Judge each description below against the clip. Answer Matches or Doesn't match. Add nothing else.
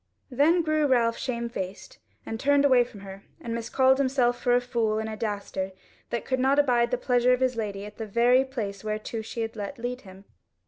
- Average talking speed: Doesn't match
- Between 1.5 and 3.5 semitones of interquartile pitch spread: Matches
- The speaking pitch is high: Matches